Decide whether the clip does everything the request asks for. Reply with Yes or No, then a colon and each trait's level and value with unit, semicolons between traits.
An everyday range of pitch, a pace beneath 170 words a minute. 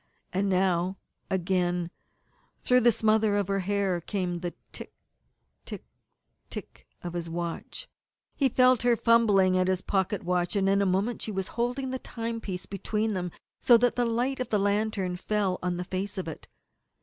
No: average, 3.8 semitones; average, 175 wpm